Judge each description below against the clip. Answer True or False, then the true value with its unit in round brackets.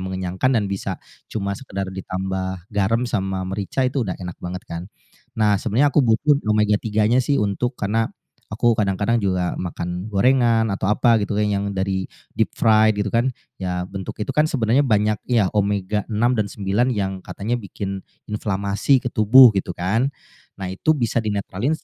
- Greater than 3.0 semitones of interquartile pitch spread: True (3.4 semitones)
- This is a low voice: True (105 Hz)